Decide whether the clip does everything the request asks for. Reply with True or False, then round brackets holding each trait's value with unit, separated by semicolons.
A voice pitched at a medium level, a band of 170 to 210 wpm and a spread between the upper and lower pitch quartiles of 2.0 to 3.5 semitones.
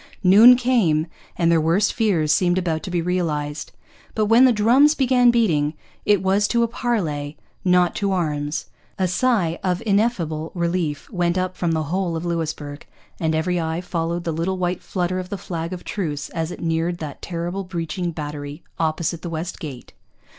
True (175 Hz; 180 wpm; 3.1 semitones)